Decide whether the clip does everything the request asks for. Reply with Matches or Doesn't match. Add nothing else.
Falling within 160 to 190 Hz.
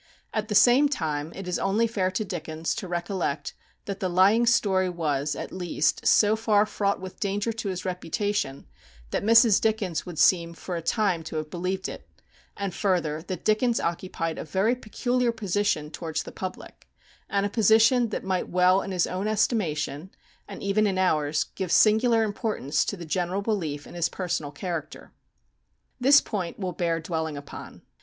Matches